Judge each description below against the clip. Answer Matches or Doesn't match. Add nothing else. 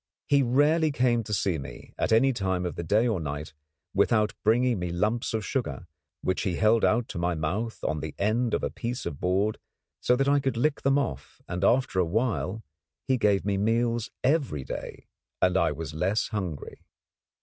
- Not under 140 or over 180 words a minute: Doesn't match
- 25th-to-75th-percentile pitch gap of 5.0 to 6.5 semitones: Matches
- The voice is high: Doesn't match